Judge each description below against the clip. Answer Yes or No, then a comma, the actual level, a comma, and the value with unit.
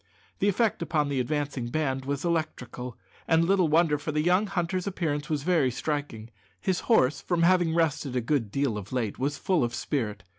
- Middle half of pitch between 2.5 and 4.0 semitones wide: No, average, 4.7 semitones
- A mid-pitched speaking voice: Yes, medium, 150 Hz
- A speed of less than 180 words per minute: No, average, 190 wpm